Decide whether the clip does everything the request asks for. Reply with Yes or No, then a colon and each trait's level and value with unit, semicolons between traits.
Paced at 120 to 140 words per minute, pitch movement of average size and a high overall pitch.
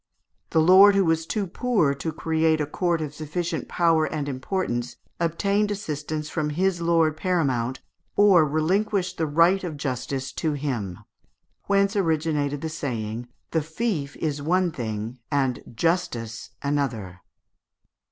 No: slow, 135 wpm; average, 4.0 semitones; medium, 155 Hz